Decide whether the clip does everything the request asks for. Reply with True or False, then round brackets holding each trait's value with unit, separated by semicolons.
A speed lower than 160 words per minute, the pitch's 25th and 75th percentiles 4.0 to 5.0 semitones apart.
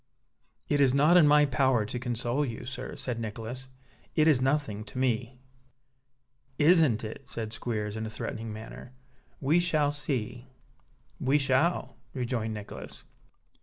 True (140 wpm; 4.3 semitones)